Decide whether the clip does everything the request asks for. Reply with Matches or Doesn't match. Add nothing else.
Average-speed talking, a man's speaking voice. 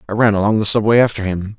Doesn't match